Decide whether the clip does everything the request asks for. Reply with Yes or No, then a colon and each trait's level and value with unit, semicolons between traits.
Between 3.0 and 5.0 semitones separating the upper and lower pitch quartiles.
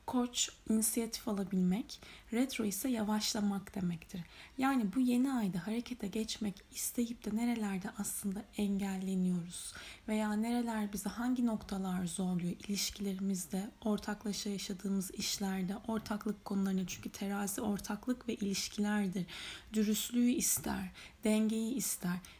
No: narrow, 2.5 semitones